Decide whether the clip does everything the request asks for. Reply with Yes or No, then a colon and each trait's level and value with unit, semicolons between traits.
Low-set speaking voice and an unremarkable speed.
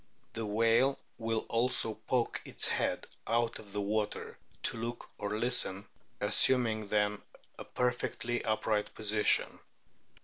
No: low, 110 Hz; slow, 125 wpm